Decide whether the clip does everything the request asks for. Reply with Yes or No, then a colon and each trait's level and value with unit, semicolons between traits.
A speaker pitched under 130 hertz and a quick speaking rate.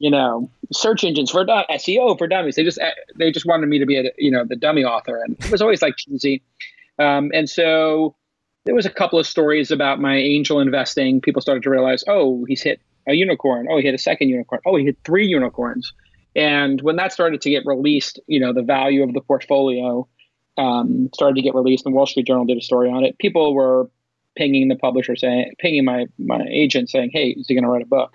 No: medium, 140 Hz; fast, 235 wpm